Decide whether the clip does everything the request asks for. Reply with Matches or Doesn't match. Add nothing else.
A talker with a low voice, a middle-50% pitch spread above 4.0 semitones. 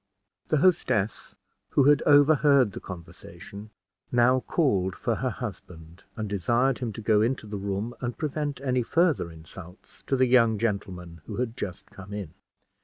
Matches